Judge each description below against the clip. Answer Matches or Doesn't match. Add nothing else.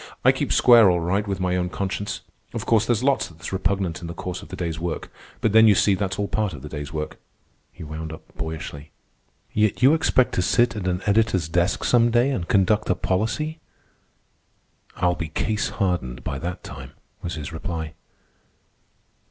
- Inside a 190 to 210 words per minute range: Matches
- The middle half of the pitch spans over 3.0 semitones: Matches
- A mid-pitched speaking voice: Doesn't match